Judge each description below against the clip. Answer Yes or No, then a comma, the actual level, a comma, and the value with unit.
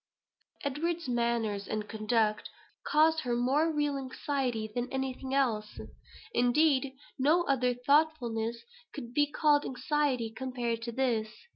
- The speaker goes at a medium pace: No, slow, 125 wpm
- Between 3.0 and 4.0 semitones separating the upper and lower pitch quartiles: Yes, average, 3.7 semitones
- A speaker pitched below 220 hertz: No, very high, 255 Hz